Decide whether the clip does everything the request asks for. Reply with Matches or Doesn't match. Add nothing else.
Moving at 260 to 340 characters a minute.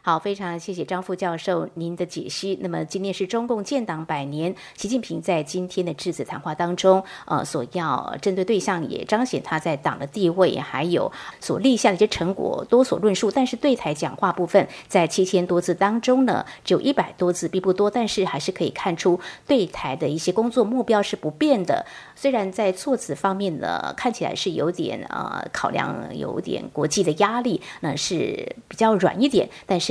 Matches